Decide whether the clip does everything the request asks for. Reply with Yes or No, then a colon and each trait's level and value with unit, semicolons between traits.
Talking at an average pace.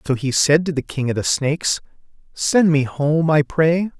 No: fast, 210 wpm